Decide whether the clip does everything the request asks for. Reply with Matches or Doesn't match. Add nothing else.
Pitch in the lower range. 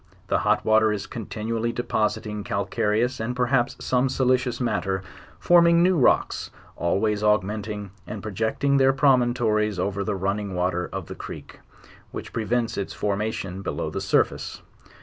Matches